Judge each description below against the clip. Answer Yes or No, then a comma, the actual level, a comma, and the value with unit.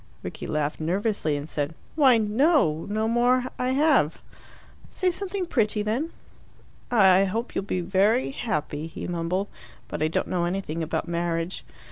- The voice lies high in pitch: Yes, high, 195 Hz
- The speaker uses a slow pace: No, average, 150 wpm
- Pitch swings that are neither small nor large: No, wide, 6.5 semitones